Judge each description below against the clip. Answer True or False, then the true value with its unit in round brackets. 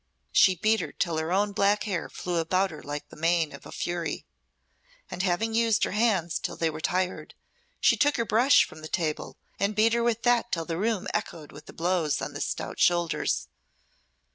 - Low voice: False (185 Hz)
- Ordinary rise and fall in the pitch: True (4.7 semitones)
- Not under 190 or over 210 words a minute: True (205 wpm)